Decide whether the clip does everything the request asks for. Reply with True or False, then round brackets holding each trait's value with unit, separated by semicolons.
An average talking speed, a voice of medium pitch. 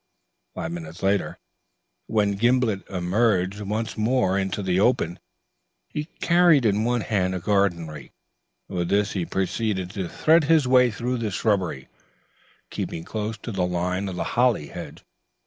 False (150 wpm; 100 Hz)